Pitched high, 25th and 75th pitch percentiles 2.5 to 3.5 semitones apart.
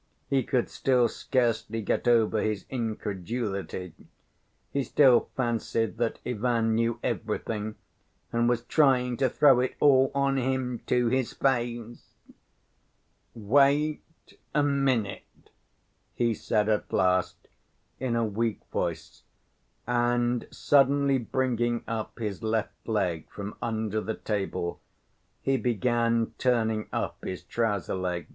No: low, 120 Hz; average, 2.9 semitones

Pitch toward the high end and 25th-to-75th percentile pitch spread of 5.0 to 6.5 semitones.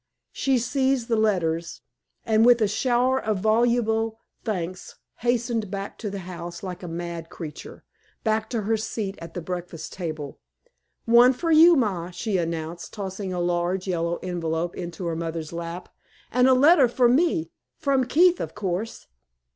Yes: high, 200 Hz; wide, 5.6 semitones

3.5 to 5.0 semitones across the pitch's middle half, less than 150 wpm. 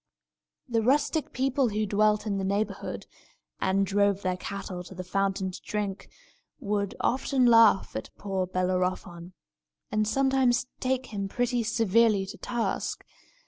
Yes: average, 3.8 semitones; average, 140 wpm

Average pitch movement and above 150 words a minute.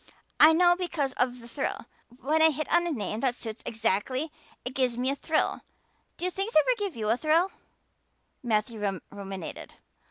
No: wide, 6.1 semitones; average, 170 wpm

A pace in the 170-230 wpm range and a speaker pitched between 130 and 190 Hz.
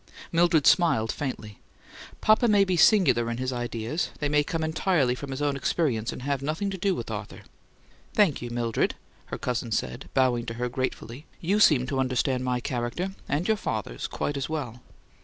Yes: average, 185 wpm; low, 135 Hz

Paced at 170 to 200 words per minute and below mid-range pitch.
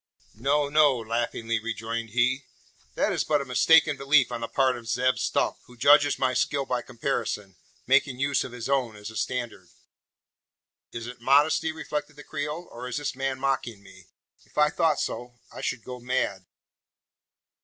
Yes: average, 175 wpm; low, 130 Hz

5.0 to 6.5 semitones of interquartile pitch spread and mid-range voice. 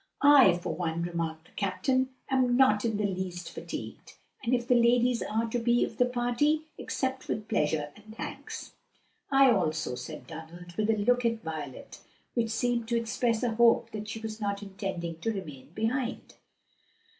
No: wide, 5.5 semitones; high, 220 Hz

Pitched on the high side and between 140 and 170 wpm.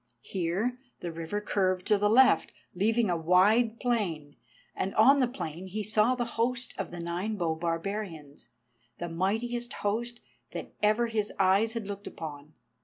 Yes: high, 205 Hz; average, 160 wpm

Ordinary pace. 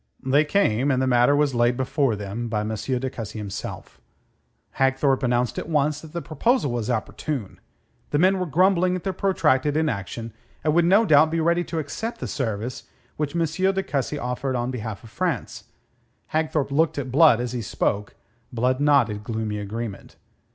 Yes: average, 180 wpm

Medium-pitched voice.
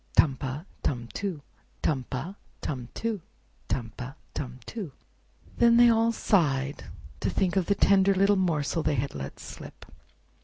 Yes: medium, 155 Hz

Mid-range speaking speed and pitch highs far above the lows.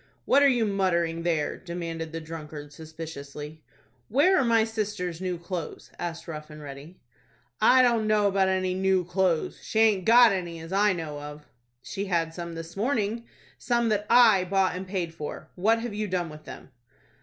No: average, 180 wpm; average, 4.4 semitones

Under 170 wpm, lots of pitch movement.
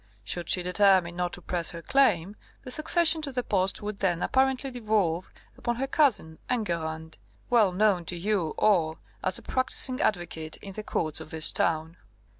No: average, 175 wpm; wide, 6.0 semitones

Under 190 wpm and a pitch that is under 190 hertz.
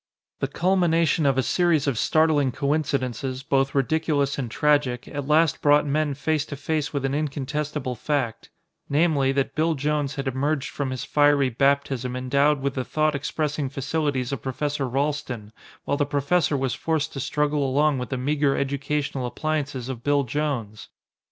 Yes: average, 165 wpm; medium, 140 Hz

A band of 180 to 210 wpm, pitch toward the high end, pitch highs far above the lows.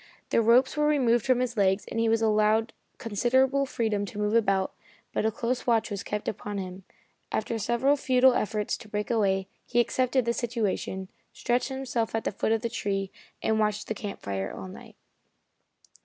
No: average, 185 wpm; high, 225 Hz; average, 2.7 semitones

